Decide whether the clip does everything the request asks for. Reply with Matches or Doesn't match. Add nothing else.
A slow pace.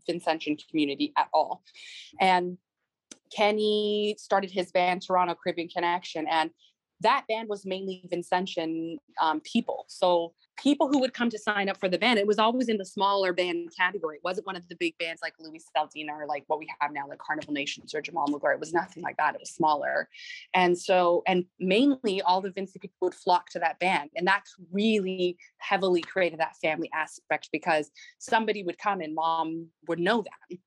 Doesn't match